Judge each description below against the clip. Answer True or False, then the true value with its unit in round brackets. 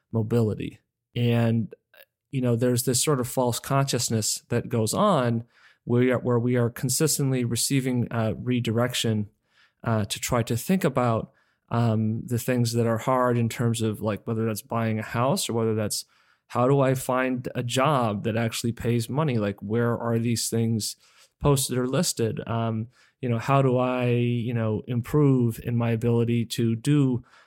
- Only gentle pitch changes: True (1.9 semitones)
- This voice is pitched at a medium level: False (120 Hz)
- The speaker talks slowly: False (165 wpm)